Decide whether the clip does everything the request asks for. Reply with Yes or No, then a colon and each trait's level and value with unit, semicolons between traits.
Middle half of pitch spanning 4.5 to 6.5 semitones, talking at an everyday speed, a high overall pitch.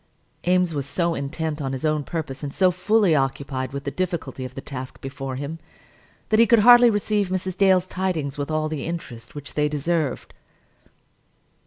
No: average, 4.8 semitones; average, 180 wpm; medium, 155 Hz